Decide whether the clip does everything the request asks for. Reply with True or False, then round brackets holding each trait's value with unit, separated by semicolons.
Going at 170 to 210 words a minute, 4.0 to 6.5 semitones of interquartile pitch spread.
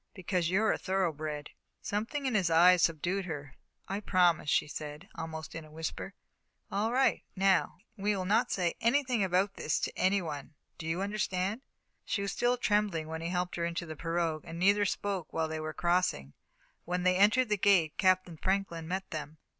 False (185 wpm; 3.6 semitones)